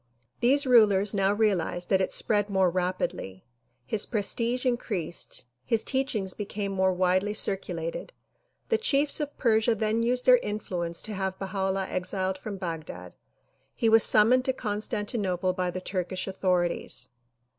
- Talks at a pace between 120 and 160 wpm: Yes, average, 145 wpm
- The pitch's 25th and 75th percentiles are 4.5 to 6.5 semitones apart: No, average, 3.4 semitones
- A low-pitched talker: No, high, 195 Hz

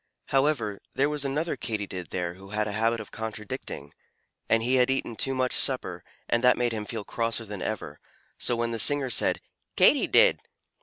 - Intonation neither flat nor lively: Yes, average, 3.5 semitones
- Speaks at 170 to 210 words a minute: Yes, average, 190 wpm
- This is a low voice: Yes, low, 115 Hz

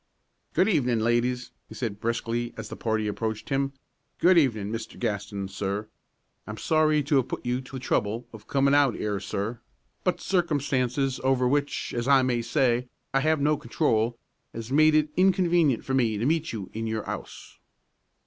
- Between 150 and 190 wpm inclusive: Yes, average, 175 wpm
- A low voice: Yes, low, 125 Hz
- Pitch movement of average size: Yes, average, 4.3 semitones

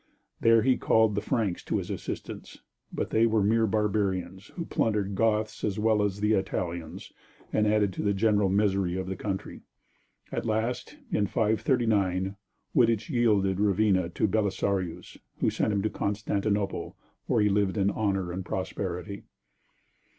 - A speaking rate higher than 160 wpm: No, average, 150 wpm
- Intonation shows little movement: Yes, narrow, 2.3 semitones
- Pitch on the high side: No, low, 105 Hz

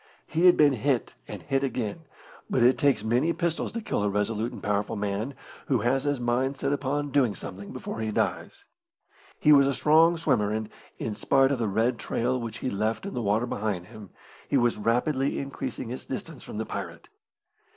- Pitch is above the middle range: No, low, 125 Hz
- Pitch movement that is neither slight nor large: Yes, average, 4.4 semitones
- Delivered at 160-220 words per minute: Yes, average, 200 wpm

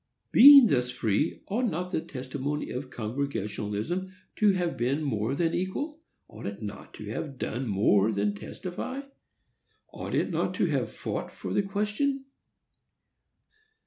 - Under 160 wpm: Yes, average, 140 wpm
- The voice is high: No, medium, 140 Hz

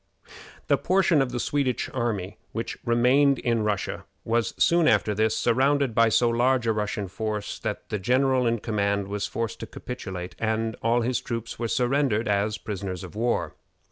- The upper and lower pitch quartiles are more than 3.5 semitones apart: No, average, 3.1 semitones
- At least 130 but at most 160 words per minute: No, average, 175 wpm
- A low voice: Yes, low, 115 Hz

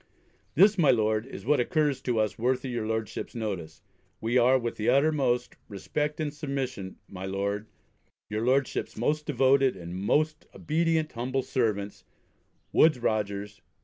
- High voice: No, low, 125 Hz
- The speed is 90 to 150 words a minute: Yes, average, 145 wpm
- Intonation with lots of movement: No, average, 4.9 semitones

